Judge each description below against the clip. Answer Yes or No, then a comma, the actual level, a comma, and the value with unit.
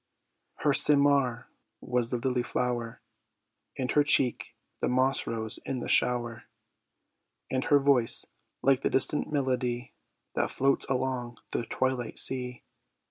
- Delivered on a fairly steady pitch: Yes, narrow, 1.9 semitones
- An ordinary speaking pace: No, slow, 130 wpm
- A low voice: Yes, low, 125 Hz